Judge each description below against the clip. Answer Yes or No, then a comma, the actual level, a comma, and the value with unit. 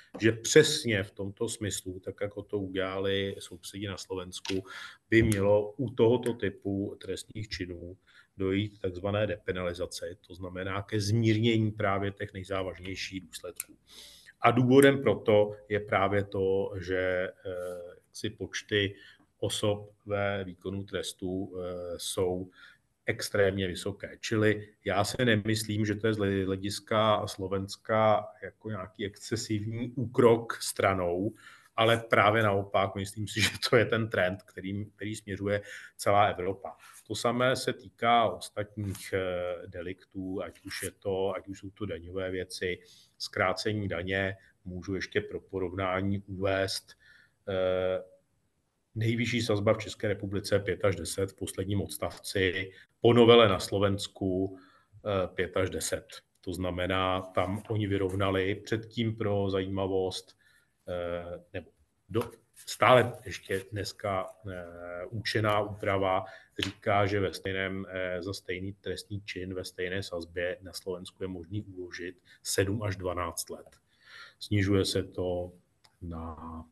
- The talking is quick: No, average, 120 wpm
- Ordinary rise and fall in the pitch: No, narrow, 2.3 semitones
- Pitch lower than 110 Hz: Yes, low, 100 Hz